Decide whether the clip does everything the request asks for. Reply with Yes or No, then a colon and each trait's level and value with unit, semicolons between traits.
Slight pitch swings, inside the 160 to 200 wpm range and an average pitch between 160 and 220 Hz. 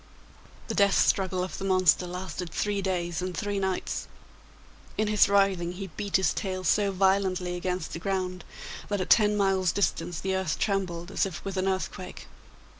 Yes: narrow, 1.5 semitones; average, 175 wpm; high, 190 Hz